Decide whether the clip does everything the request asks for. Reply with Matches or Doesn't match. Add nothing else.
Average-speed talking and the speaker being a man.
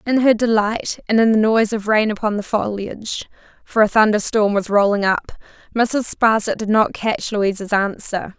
Doesn't match